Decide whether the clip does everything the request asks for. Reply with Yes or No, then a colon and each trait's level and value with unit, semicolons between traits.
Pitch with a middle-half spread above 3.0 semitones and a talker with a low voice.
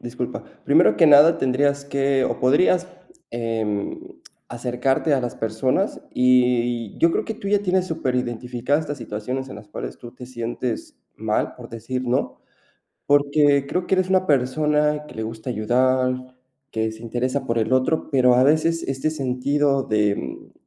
Yes: average, 3.5 semitones; low, 130 Hz